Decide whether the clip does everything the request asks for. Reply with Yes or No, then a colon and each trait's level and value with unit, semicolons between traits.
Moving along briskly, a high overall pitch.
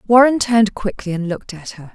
Yes: fast, 215 wpm; high, 205 Hz